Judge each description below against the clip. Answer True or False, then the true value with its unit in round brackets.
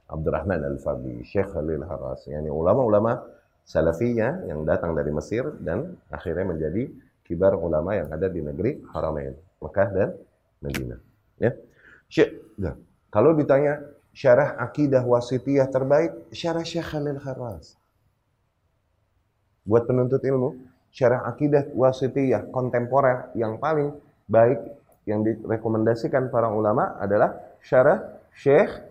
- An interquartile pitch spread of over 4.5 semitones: True (5.0 semitones)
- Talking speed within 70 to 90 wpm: False (110 wpm)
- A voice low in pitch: True (115 Hz)